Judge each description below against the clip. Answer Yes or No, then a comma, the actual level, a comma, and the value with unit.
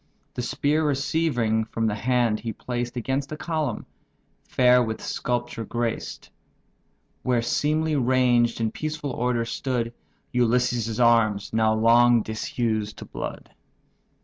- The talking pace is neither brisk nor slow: No, slow, 120 wpm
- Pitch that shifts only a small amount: Yes, narrow, 2.2 semitones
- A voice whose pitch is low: Yes, low, 120 Hz